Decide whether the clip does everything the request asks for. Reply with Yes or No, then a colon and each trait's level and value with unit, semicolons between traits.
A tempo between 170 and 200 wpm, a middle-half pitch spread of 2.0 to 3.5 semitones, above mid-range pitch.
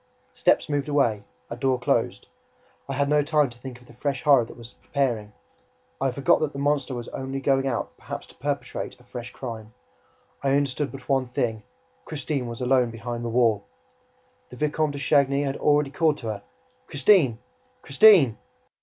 No: average, 180 wpm; average, 3.1 semitones; low, 135 Hz